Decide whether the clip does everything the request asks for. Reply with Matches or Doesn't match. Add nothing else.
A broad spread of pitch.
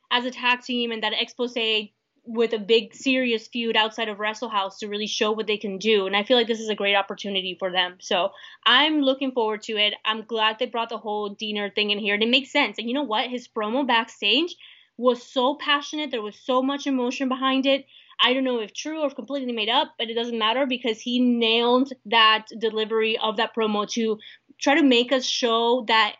Doesn't match